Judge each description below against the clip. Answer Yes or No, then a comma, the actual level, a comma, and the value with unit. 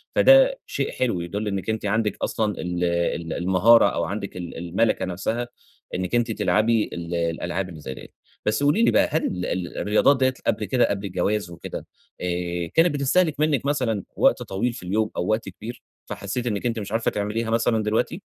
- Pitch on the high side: No, low, 105 Hz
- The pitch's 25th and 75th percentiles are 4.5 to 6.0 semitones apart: Yes, average, 4.9 semitones